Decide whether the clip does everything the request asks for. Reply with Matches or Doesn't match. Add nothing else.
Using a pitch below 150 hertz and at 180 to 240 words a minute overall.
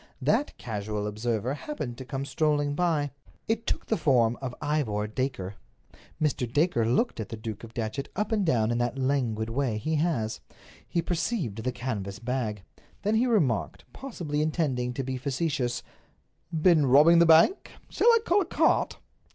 Doesn't match